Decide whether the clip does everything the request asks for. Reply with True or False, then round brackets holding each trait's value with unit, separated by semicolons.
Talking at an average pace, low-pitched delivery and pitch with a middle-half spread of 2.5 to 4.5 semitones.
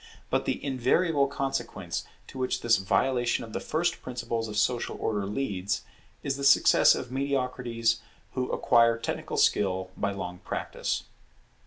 True (145 wpm; 120 Hz; 4.1 semitones)